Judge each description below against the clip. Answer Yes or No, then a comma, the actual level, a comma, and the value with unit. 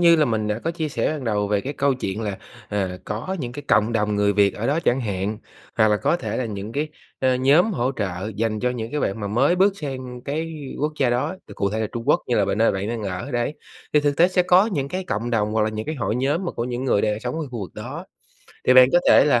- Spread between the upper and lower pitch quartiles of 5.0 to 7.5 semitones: Yes, wide, 5.5 semitones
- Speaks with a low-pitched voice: Yes, low, 120 Hz